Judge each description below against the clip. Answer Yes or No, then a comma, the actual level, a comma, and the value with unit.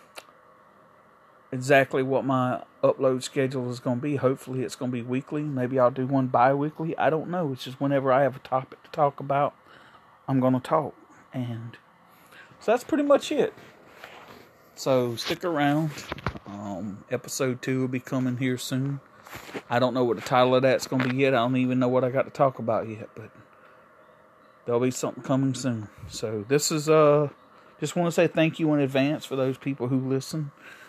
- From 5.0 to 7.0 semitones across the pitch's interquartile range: No, narrow, 2.5 semitones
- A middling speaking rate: Yes, average, 185 wpm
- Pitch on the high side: No, low, 130 Hz